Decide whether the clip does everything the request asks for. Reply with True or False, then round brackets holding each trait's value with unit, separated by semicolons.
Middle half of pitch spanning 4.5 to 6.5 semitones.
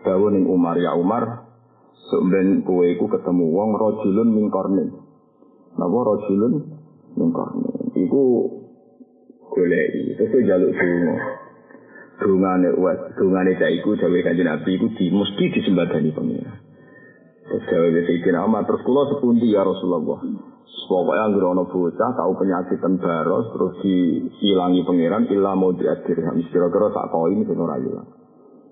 True (4.9 semitones)